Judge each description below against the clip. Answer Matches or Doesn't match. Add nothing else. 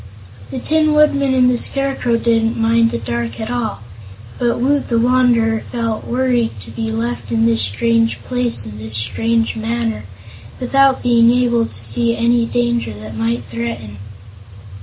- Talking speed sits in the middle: Matches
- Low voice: Doesn't match